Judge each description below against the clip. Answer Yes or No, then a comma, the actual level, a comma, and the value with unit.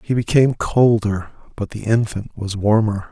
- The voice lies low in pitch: Yes, low, 110 Hz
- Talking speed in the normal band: Yes, average, 155 wpm